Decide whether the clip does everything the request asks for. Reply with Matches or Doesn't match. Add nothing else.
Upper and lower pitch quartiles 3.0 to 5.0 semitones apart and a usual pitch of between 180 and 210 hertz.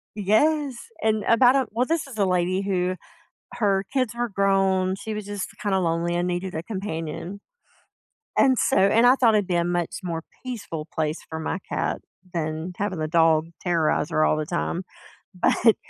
Matches